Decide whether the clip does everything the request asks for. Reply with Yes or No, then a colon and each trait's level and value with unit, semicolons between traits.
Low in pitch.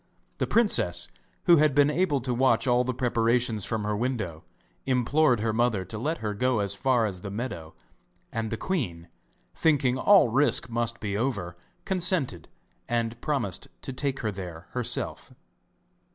Yes: low, 120 Hz